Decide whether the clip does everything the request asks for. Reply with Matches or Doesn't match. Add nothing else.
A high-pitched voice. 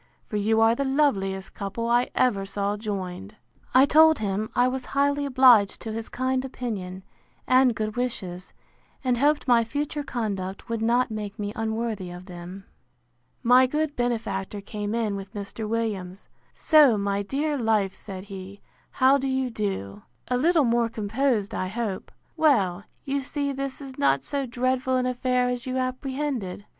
Matches